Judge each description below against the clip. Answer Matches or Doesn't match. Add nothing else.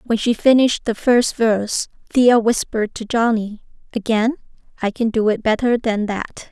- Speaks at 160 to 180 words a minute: Matches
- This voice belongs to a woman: Matches